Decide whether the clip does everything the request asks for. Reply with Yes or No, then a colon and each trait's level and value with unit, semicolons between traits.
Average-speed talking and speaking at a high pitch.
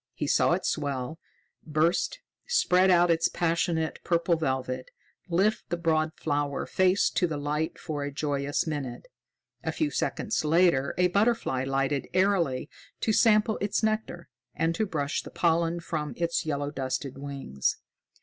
No: average, 150 wpm; medium, 160 Hz